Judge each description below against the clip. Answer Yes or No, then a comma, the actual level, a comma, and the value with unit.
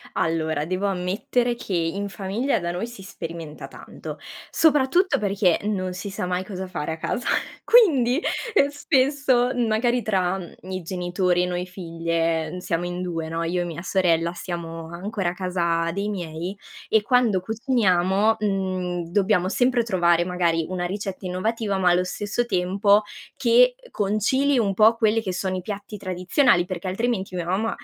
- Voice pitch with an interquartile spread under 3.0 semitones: No, average, 3.8 semitones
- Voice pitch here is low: No, high, 190 Hz